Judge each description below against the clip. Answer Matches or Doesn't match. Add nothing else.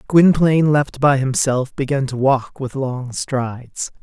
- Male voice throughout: Matches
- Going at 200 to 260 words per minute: Doesn't match